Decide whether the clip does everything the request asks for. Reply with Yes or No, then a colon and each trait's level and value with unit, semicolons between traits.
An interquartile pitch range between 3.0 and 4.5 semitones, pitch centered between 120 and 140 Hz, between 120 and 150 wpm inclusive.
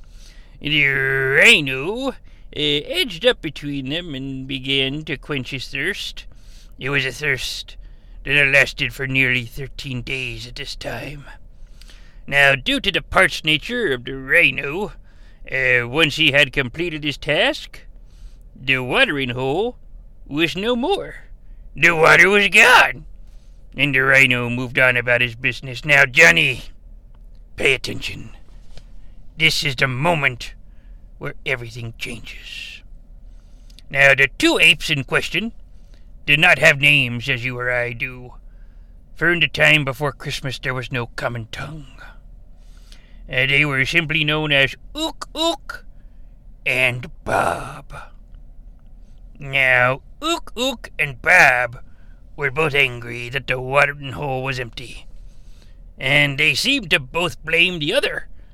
Yes: average, 3.7 semitones; low, 135 Hz; slow, 135 wpm